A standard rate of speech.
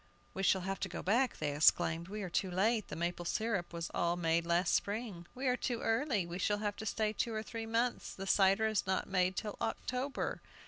No: fast, 225 wpm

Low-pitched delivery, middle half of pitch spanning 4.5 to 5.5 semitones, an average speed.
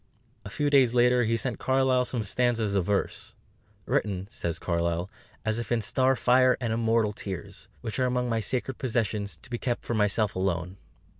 No: low, 115 Hz; average, 3.7 semitones; average, 180 wpm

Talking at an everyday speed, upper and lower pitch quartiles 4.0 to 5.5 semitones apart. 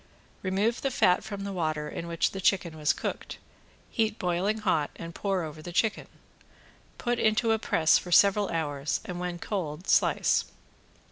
Yes: average, 165 wpm; average, 4.3 semitones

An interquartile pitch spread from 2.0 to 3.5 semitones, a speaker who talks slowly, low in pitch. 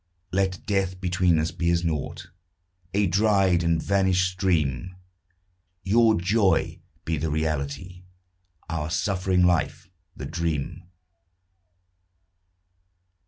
Yes: average, 2.8 semitones; slow, 100 wpm; very low, 90 Hz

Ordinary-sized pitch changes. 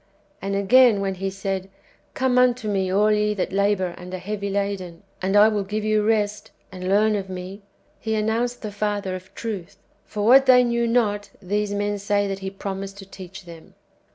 No: narrow, 1.8 semitones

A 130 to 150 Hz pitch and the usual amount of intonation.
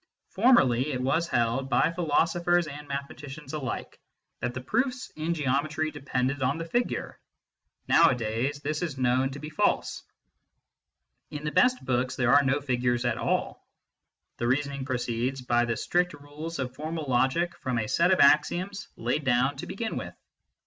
Yes: medium, 140 Hz; average, 4.3 semitones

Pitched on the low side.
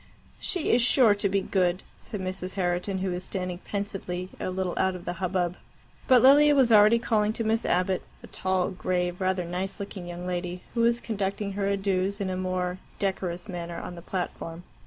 No: high, 190 Hz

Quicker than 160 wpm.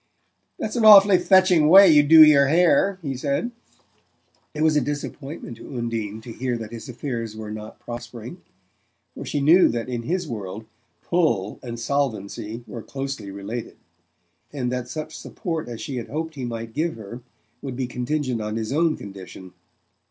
Yes: average, 170 wpm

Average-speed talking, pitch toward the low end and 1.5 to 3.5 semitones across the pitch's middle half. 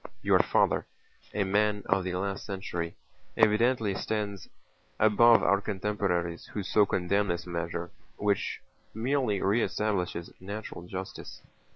No: slow, 125 wpm; low, 100 Hz; average, 2.8 semitones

